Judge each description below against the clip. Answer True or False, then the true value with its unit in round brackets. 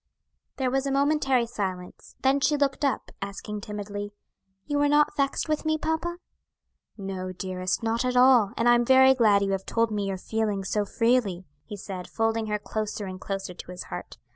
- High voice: True (220 Hz)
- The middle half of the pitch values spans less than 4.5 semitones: False (5.2 semitones)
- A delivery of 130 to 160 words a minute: False (190 wpm)